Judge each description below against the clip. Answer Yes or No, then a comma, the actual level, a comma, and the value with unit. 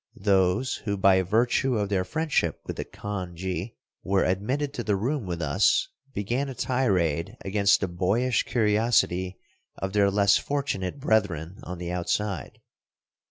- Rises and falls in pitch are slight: No, average, 4.6 semitones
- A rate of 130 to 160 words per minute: Yes, average, 145 wpm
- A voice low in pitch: Yes, low, 100 Hz